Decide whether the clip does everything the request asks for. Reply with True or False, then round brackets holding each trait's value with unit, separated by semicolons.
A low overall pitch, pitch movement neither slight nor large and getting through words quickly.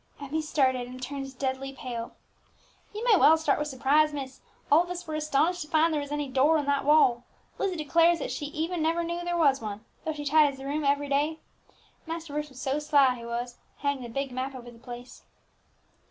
False (285 Hz; 3.0 semitones; 220 wpm)